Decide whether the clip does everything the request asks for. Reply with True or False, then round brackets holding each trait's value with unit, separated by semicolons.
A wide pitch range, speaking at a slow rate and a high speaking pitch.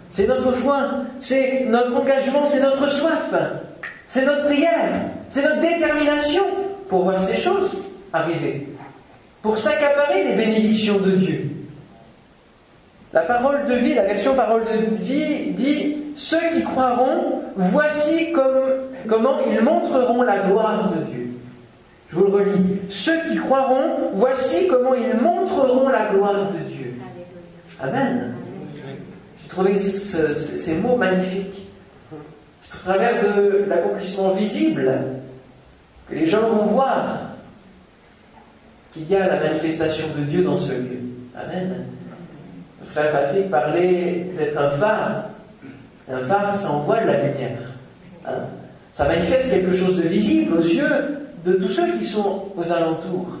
True (7.7 semitones; 135 wpm; 200 Hz)